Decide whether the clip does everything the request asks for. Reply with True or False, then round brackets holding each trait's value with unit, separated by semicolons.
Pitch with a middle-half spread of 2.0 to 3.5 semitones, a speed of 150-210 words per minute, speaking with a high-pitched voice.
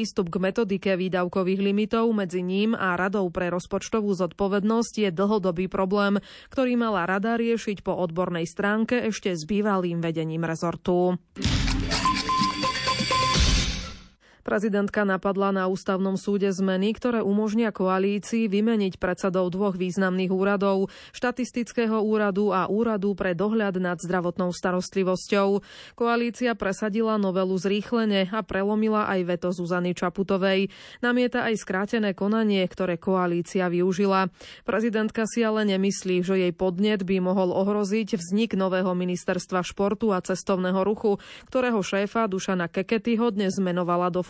False (2.6 semitones; 125 wpm; 195 Hz)